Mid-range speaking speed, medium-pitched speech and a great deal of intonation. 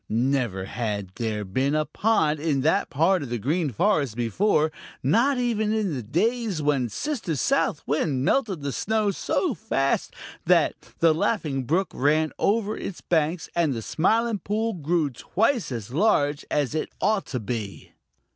Yes: average, 160 wpm; medium, 155 Hz; wide, 7.9 semitones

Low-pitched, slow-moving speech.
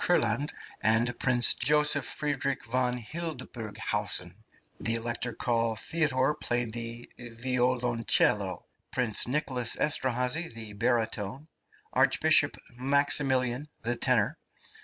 Yes: low, 125 Hz; slow, 95 wpm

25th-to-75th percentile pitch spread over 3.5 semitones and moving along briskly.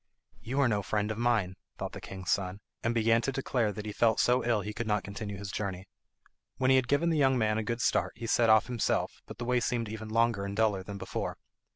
No: average, 2.7 semitones; fast, 245 wpm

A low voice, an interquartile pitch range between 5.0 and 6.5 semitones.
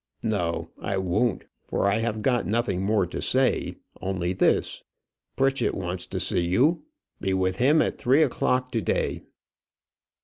Yes: low, 105 Hz; wide, 5.4 semitones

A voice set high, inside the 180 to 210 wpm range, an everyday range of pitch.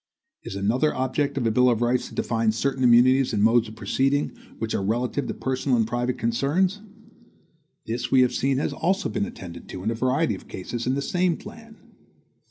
No: low, 125 Hz; average, 200 wpm; average, 3.4 semitones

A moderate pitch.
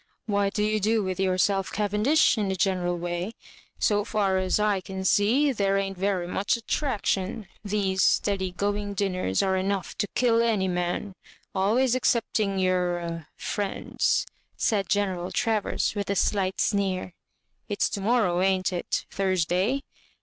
No: high, 195 Hz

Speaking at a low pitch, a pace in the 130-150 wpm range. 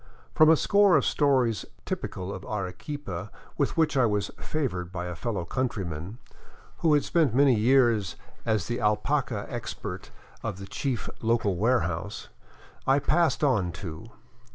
Yes: low, 115 Hz; average, 145 wpm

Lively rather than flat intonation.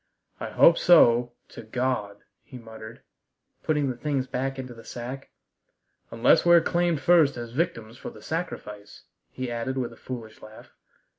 No: average, 3.7 semitones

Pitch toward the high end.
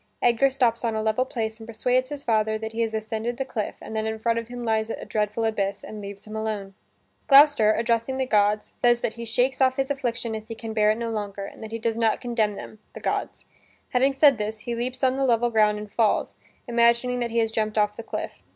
Yes: high, 225 Hz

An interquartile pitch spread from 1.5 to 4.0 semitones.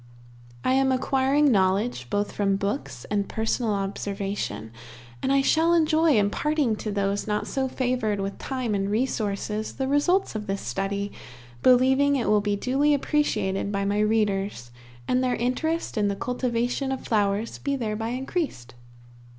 No: average, 4.9 semitones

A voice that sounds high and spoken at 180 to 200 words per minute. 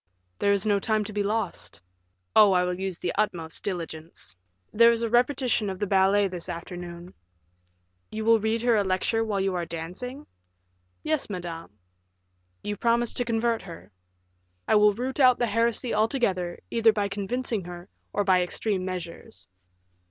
No: high, 205 Hz; average, 165 wpm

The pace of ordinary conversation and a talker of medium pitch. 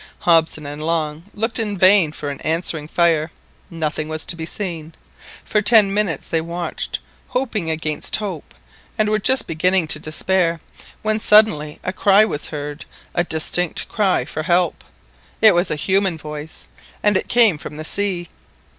Yes: average, 160 wpm; medium, 170 Hz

